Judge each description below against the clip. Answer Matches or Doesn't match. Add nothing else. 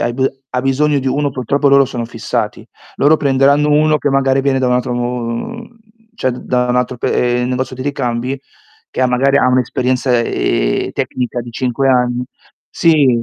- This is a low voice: Matches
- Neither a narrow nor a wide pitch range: Doesn't match